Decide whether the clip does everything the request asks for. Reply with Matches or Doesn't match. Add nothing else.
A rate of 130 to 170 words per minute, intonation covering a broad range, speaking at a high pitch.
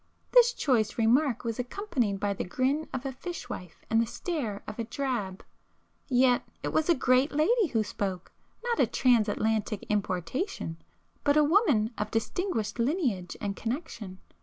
Matches